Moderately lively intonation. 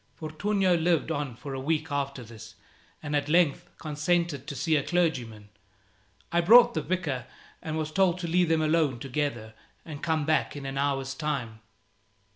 Yes: average, 3.7 semitones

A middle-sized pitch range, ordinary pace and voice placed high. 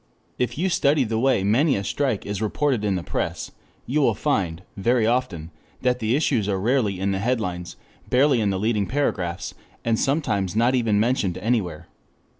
No: average, 4.7 semitones; average, 185 wpm; low, 110 Hz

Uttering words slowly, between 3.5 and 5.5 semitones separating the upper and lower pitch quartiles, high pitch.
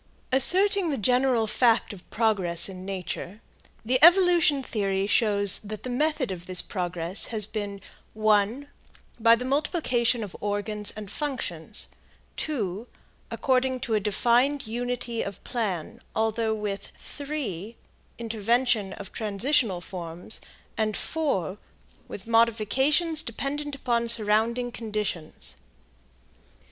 Yes: slow, 115 wpm; average, 4.1 semitones; high, 225 Hz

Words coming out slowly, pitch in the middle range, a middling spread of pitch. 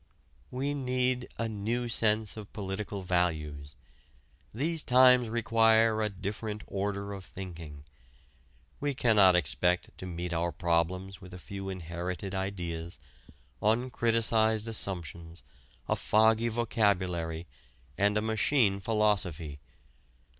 No: slow, 110 wpm; low, 100 Hz; average, 4.1 semitones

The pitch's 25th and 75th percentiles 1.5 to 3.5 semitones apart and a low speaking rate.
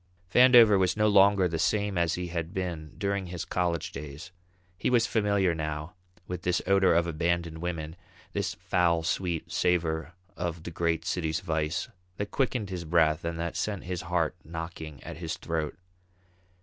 No: narrow, 2.5 semitones; average, 165 wpm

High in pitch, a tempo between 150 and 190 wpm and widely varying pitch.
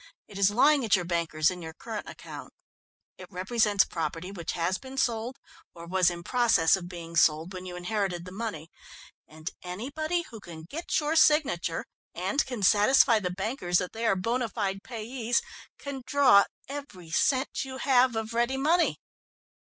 Yes: high, 205 Hz; average, 170 wpm; wide, 6.2 semitones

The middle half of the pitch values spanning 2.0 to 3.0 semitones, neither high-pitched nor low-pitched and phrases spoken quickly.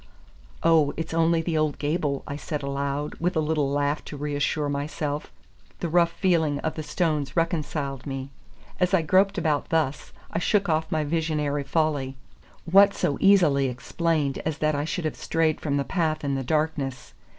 No: narrow, 2.5 semitones; medium, 155 Hz; average, 175 wpm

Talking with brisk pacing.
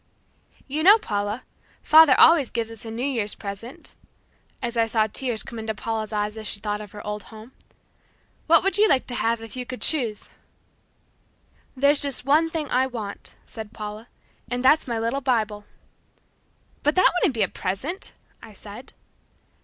No: average, 175 wpm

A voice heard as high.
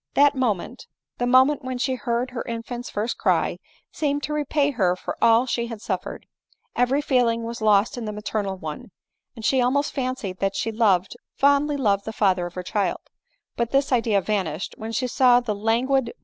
Yes: high, 235 Hz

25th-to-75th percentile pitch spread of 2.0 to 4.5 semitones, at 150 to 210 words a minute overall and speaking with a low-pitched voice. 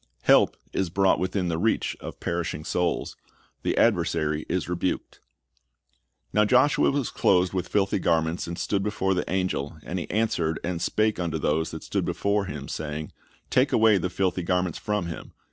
Yes: average, 3.1 semitones; average, 170 wpm; very low, 90 Hz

